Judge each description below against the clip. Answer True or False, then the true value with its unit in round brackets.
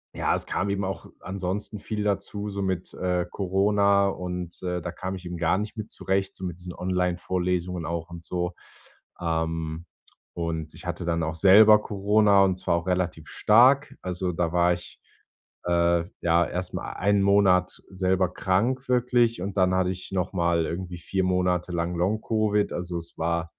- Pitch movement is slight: True (2.3 semitones)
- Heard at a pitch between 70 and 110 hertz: True (90 Hz)